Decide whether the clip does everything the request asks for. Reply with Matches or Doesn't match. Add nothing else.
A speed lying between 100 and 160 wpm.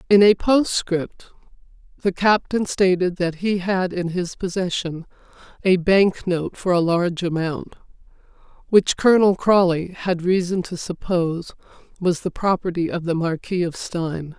Matches